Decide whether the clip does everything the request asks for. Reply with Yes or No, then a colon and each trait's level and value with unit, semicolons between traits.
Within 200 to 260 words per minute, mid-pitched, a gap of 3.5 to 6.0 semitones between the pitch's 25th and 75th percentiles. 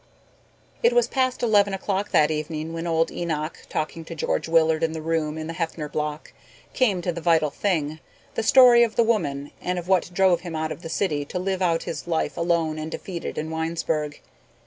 No: fast, 205 wpm; medium, 165 Hz; average, 3.1 semitones